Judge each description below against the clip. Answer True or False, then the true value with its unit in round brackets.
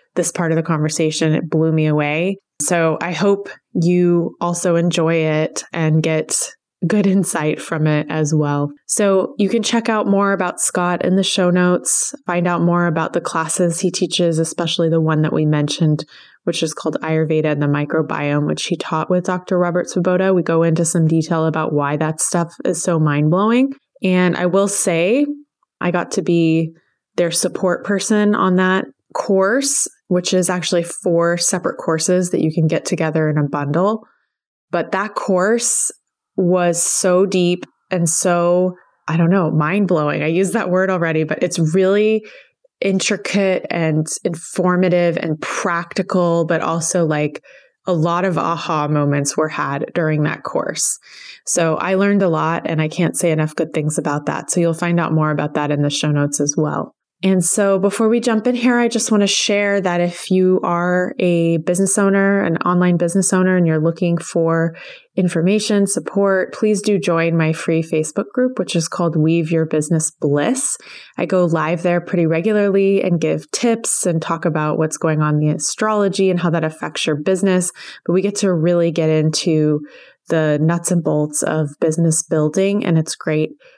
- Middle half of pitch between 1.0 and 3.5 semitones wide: True (2.9 semitones)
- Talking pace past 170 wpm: True (180 wpm)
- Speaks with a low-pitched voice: False (175 Hz)